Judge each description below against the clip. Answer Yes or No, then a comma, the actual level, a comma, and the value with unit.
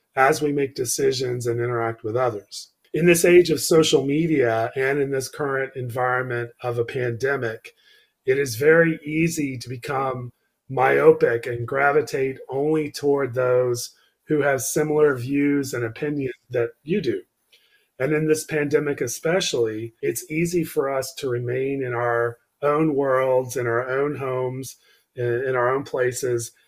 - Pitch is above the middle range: No, low, 135 Hz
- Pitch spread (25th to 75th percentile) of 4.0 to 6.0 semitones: No, average, 3.6 semitones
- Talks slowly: No, average, 150 wpm